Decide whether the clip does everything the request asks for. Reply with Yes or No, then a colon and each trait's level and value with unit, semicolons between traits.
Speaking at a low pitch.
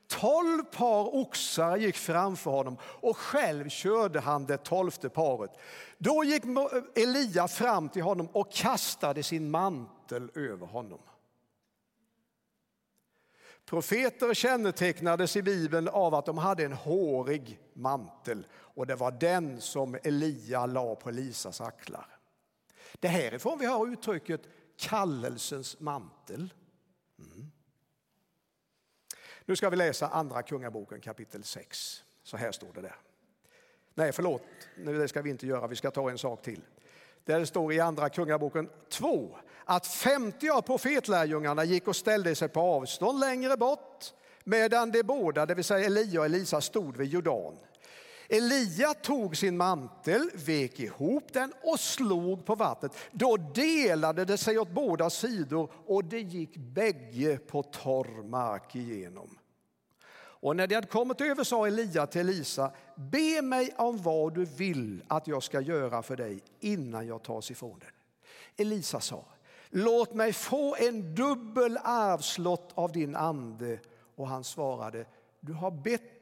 No: medium, 175 Hz